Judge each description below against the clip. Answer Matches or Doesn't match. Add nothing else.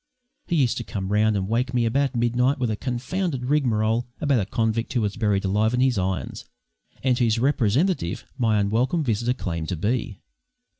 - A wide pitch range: Doesn't match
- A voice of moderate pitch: Doesn't match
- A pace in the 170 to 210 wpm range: Matches